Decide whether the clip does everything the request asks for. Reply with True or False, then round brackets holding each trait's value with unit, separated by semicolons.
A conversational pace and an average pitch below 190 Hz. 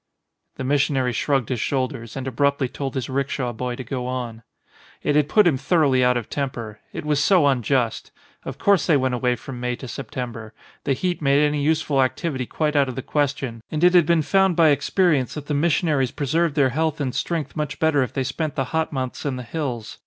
False (220 wpm; 140 Hz)